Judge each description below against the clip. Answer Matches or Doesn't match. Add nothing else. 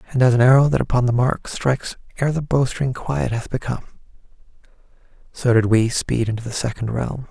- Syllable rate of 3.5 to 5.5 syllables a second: Doesn't match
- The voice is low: Matches